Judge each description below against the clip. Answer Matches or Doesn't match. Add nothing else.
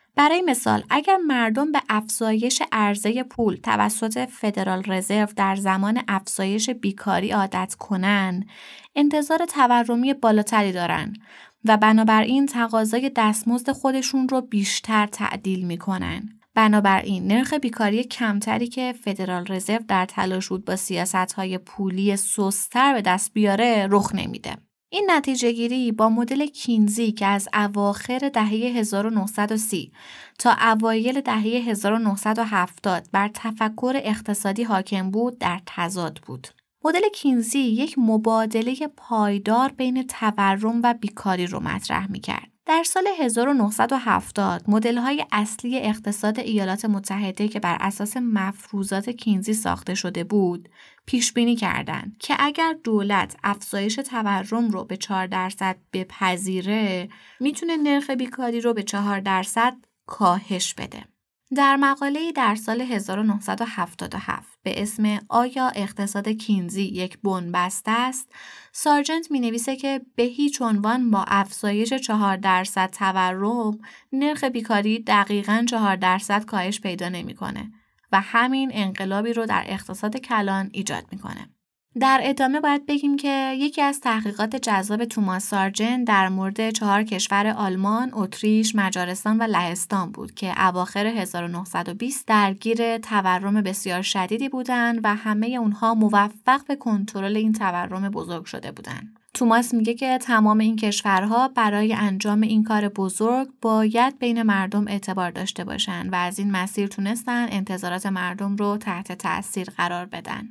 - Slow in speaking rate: Doesn't match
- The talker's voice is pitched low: Doesn't match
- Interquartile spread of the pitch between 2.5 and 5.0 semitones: Matches